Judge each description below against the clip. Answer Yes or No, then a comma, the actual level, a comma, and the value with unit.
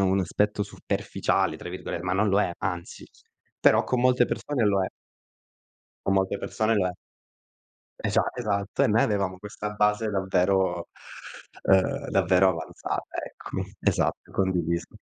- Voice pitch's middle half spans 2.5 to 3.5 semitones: No, narrow, 2.0 semitones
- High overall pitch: No, very low, 95 Hz